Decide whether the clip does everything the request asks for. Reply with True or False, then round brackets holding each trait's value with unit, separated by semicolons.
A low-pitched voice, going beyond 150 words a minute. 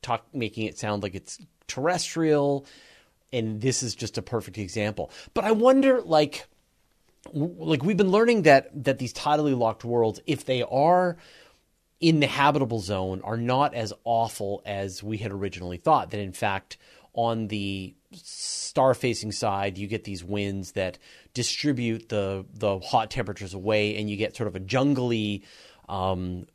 True (115 Hz; 165 wpm)